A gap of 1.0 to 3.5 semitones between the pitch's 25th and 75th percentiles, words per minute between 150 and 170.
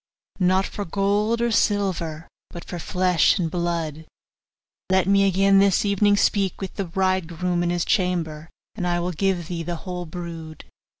Yes: narrow, 2.5 semitones; average, 165 wpm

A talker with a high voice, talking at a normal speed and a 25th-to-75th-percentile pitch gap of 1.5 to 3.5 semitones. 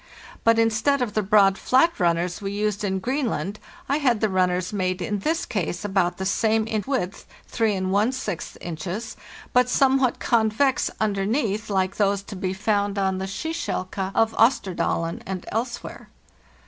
Yes: high, 205 Hz; average, 150 wpm; average, 3.2 semitones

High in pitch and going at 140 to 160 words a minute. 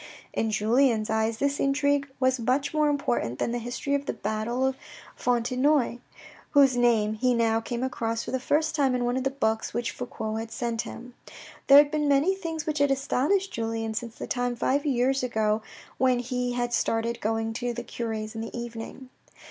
No: high, 245 Hz; average, 195 wpm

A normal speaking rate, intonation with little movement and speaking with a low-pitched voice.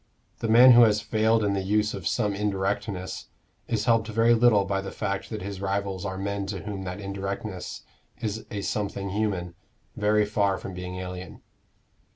Yes: average, 180 wpm; narrow, 1.8 semitones; low, 100 Hz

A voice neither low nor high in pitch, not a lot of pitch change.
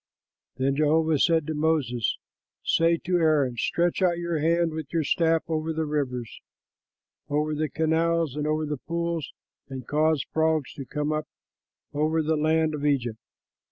Yes: medium, 155 Hz; narrow, 1.7 semitones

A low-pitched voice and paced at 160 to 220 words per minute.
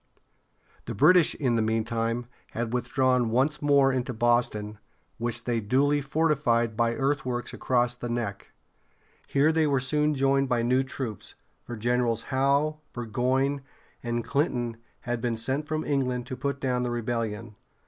No: low, 125 Hz; average, 150 wpm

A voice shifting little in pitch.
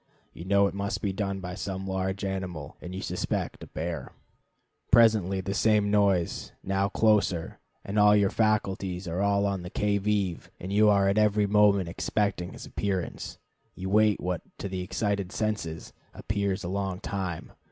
Yes: narrow, 1.8 semitones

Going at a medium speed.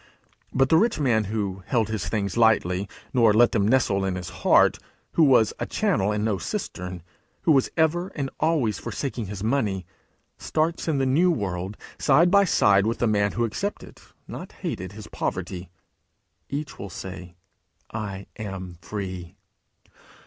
Yes: average, 160 wpm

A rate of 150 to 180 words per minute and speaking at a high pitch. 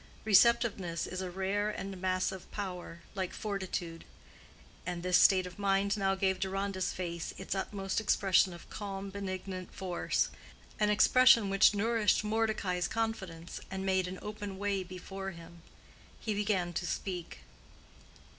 No: slow, 135 wpm; high, 195 Hz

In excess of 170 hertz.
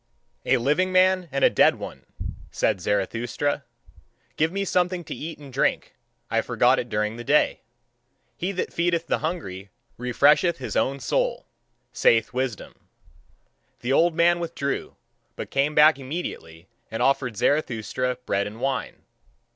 No: medium, 140 Hz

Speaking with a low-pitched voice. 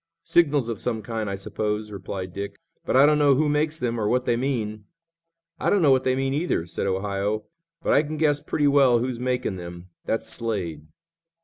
Yes: low, 115 Hz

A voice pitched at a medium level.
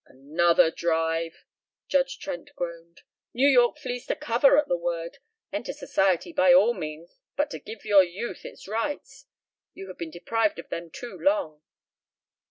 No: high, 195 Hz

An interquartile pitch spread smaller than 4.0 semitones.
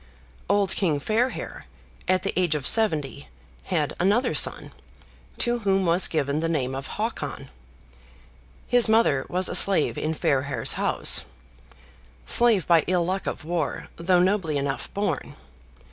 No: average, 5.2 semitones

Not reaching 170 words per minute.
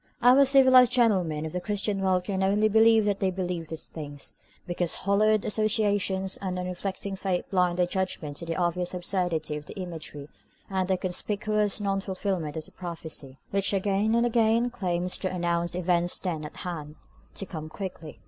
No: average, 175 wpm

